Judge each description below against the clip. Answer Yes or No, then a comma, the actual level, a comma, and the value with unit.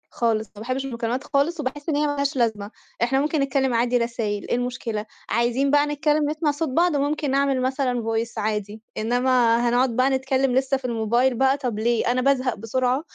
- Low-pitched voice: No, very high, 255 Hz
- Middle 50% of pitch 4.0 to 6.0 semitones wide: No, average, 3.0 semitones